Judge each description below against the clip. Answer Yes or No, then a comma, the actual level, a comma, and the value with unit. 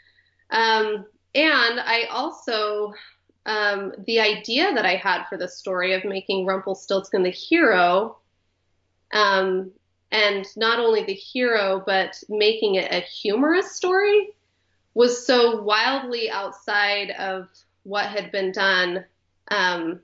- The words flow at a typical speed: No, slow, 120 wpm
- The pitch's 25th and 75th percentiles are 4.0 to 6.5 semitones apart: No, average, 3.4 semitones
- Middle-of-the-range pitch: No, high, 205 Hz